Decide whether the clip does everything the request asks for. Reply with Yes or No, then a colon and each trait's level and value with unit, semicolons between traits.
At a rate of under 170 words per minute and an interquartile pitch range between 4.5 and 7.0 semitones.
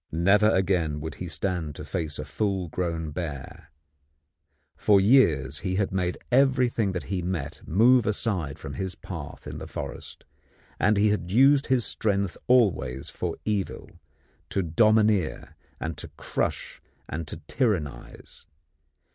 Yes: average, 140 wpm; average, 5.1 semitones